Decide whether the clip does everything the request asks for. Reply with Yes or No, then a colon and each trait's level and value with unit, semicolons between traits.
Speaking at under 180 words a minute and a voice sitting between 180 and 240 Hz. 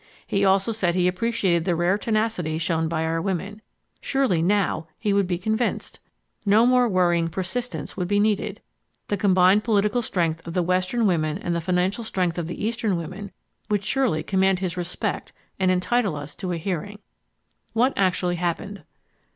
Yes: average, 170 wpm; medium, 185 Hz